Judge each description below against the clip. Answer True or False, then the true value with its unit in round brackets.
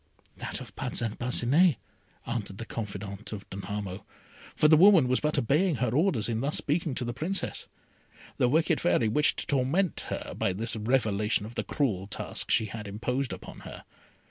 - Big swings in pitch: True (5.8 semitones)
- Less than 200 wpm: True (175 wpm)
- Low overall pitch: True (120 Hz)